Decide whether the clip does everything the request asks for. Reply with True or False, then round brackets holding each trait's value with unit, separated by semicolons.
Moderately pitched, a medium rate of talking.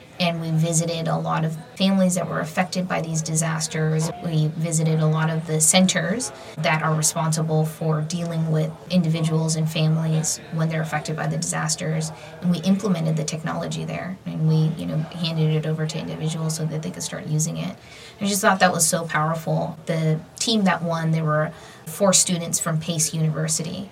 True (160 Hz; 190 wpm)